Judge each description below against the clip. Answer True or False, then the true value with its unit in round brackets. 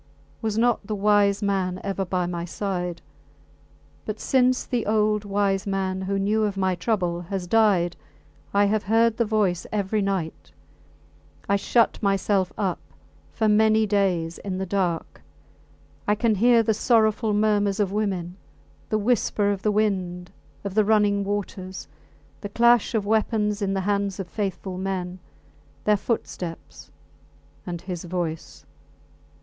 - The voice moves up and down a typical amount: False (2.3 semitones)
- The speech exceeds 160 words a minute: False (145 wpm)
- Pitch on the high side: True (200 Hz)